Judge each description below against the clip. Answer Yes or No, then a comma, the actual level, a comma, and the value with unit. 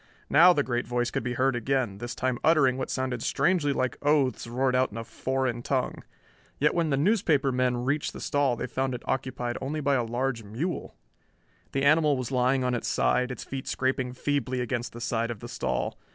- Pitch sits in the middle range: No, low, 130 Hz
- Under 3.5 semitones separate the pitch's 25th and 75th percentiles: Yes, narrow, 2.4 semitones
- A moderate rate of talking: No, fast, 210 wpm